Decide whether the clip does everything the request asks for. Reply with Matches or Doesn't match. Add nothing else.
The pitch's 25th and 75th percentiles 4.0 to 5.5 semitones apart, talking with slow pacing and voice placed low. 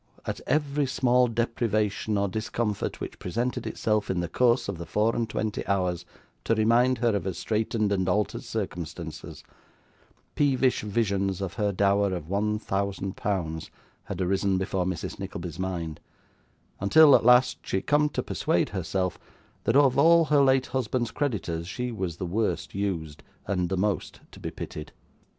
Doesn't match